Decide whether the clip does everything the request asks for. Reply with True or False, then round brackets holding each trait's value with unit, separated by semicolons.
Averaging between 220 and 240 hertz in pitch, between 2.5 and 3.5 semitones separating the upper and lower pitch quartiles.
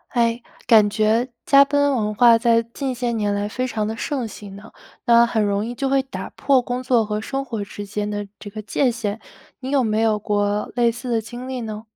True (230 Hz; 2.9 semitones)